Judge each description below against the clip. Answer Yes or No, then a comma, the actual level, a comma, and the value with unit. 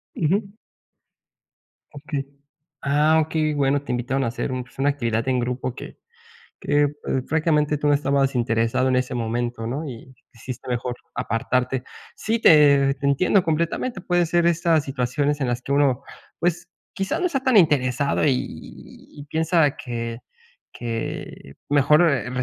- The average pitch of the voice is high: No, medium, 140 Hz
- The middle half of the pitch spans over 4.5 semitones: No, average, 3.9 semitones